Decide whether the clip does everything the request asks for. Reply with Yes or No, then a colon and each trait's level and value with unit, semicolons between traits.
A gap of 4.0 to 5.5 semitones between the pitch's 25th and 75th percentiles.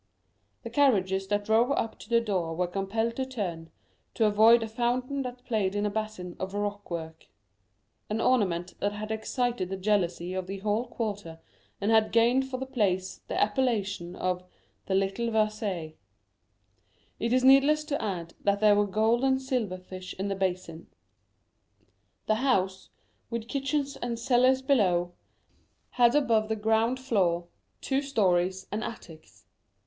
Yes: average, 4.3 semitones